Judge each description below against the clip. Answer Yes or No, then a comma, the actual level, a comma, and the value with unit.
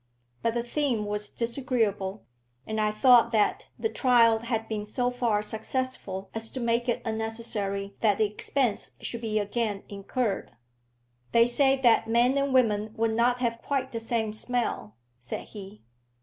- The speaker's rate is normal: Yes, average, 160 wpm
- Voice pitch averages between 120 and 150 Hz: No, high, 230 Hz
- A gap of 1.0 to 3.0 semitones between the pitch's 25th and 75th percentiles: Yes, narrow, 2.6 semitones